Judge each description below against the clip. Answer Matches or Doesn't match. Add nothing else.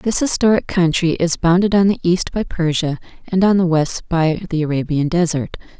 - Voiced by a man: Doesn't match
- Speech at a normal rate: Matches